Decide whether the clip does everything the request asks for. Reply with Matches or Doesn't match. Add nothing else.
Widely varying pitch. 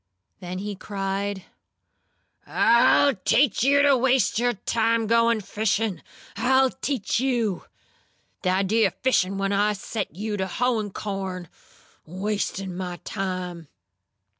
Doesn't match